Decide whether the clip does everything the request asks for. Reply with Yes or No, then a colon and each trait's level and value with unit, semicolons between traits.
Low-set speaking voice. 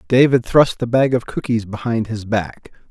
Yes: low, 115 Hz